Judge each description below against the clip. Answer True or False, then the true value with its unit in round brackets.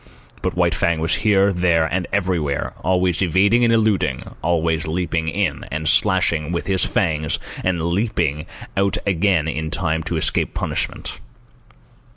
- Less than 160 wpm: True (150 wpm)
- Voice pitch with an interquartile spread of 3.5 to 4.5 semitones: False (3.1 semitones)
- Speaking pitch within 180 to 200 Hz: False (85 Hz)